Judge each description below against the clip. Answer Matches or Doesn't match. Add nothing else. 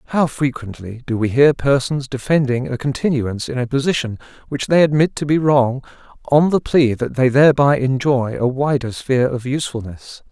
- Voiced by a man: Matches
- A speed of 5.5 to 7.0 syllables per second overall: Doesn't match